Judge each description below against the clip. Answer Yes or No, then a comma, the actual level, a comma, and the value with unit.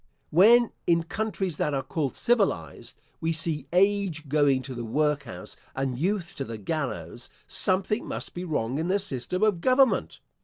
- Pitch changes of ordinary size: No, wide, 6.4 semitones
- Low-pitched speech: No, medium, 160 Hz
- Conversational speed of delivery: Yes, average, 160 wpm